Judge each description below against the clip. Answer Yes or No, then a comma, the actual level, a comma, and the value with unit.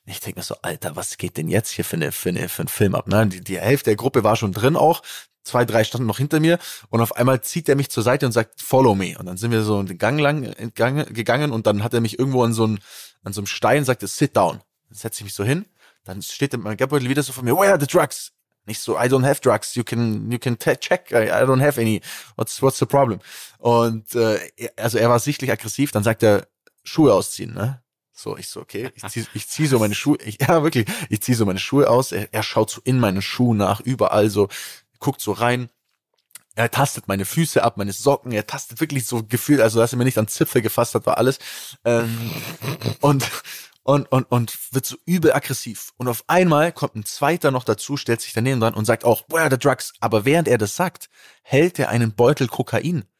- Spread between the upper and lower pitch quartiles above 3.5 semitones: Yes, average, 4.1 semitones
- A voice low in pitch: Yes, low, 120 Hz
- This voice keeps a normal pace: No, fast, 240 wpm